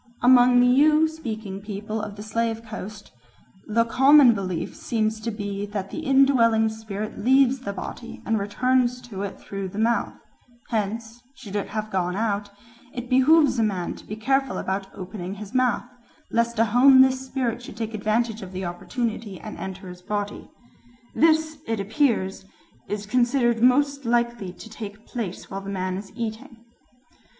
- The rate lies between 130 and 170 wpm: Yes, average, 165 wpm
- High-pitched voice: Yes, high, 220 Hz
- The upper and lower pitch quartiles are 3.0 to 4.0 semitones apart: Yes, average, 3.6 semitones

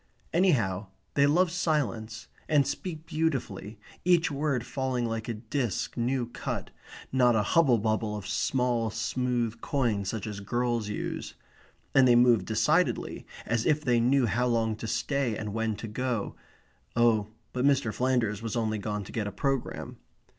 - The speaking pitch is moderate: No, low, 120 Hz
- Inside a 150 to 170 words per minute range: Yes, average, 160 wpm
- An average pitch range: Yes, average, 3.6 semitones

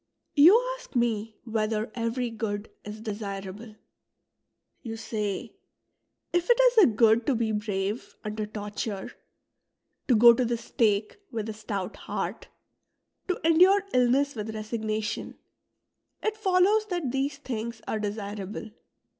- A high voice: Yes, high, 225 Hz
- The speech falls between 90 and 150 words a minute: Yes, slow, 135 wpm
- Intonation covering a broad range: No, average, 3.9 semitones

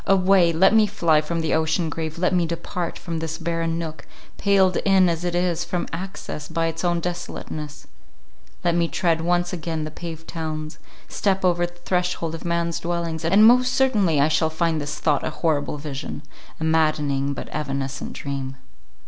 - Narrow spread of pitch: Yes, narrow, 2.1 semitones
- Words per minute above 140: Yes, average, 175 wpm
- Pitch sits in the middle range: Yes, medium, 165 Hz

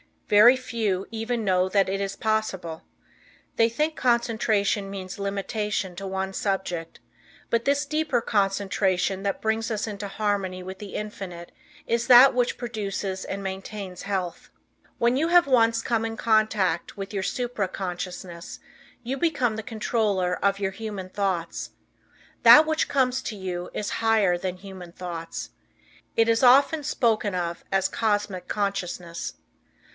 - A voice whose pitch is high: Yes, high, 205 Hz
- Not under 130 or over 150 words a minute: Yes, average, 145 wpm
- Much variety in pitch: No, average, 3.3 semitones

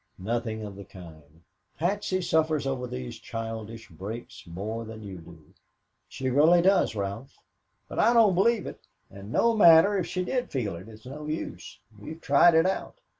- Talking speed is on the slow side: No, average, 175 wpm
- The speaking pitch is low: Yes, low, 120 Hz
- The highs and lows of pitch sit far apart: Yes, wide, 8.9 semitones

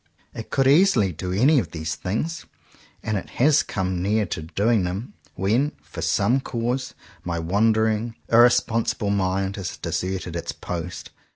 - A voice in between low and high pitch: No, low, 105 Hz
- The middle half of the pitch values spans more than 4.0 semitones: Yes, average, 4.6 semitones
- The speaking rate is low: No, average, 155 wpm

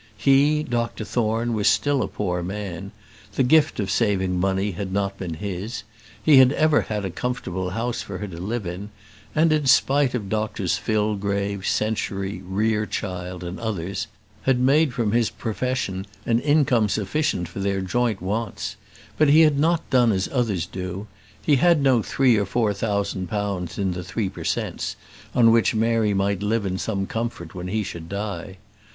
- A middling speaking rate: Yes, average, 175 wpm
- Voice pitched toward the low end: Yes, low, 105 Hz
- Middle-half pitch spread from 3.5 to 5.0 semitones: Yes, average, 4.1 semitones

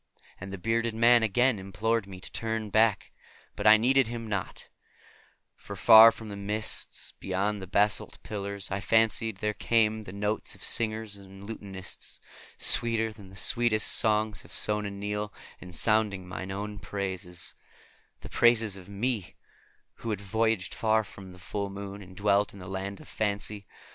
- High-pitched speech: No, low, 105 Hz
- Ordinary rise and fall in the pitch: No, narrow, 2.2 semitones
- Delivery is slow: No, average, 165 wpm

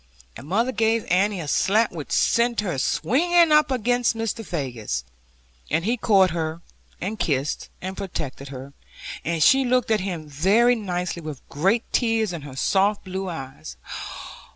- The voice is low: No, high, 190 Hz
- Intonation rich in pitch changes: Yes, wide, 6.4 semitones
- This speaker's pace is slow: No, average, 155 wpm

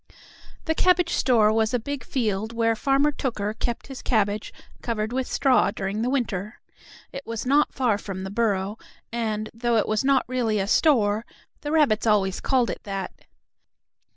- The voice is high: Yes, high, 230 Hz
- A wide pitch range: No, average, 3.8 semitones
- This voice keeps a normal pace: Yes, average, 170 wpm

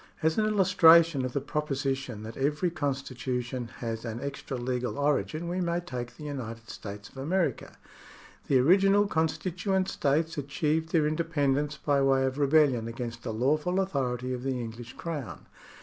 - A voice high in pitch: No, medium, 140 Hz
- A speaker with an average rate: Yes, average, 160 wpm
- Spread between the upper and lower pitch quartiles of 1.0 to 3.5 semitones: No, average, 4.5 semitones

